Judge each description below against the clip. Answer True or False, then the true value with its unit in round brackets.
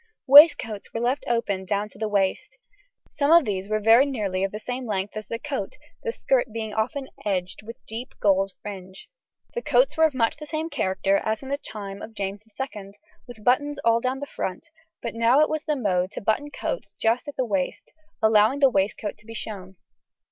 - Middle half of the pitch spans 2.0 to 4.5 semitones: False (5.0 semitones)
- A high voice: True (225 Hz)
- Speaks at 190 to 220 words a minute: True (205 wpm)